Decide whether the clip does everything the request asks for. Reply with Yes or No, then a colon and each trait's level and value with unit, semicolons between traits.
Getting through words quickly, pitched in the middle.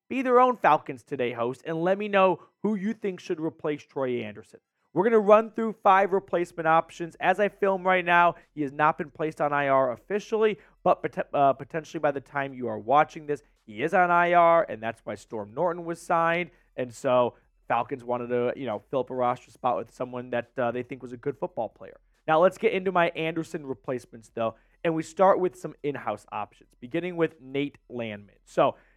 Yes: fast, 210 wpm; medium, 160 Hz